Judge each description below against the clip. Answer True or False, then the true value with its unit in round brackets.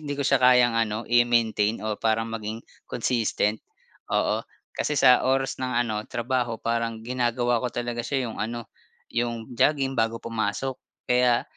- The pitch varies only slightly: True (1.9 semitones)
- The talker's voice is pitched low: True (120 Hz)